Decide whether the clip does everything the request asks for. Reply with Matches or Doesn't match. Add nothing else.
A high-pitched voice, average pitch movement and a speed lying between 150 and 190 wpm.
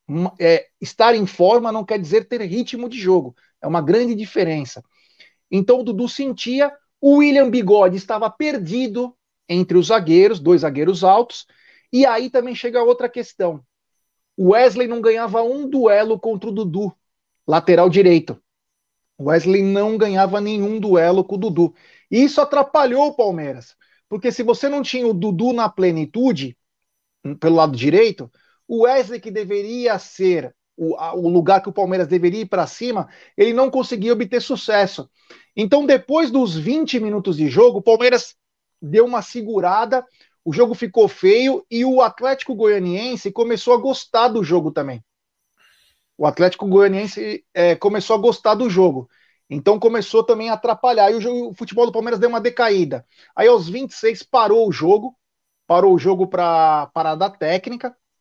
Matches